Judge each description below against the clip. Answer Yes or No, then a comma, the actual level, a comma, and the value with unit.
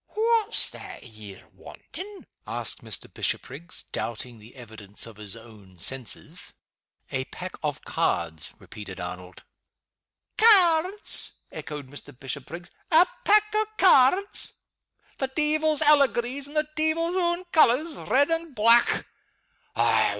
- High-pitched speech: Yes, very high, 265 Hz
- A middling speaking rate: No, slow, 115 wpm